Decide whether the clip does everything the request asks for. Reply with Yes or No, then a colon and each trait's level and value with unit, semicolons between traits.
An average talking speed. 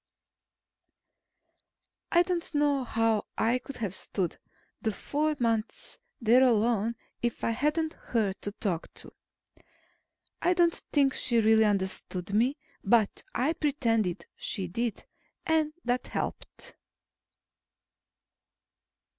No: slow, 110 wpm